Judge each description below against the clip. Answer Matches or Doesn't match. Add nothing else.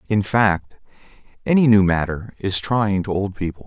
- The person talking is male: Matches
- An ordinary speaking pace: Matches